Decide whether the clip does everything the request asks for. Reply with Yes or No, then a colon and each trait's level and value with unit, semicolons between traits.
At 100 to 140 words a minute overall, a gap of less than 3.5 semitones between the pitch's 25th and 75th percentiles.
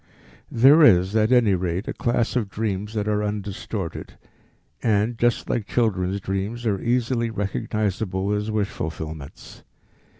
Yes: slow, 135 wpm; average, 3.1 semitones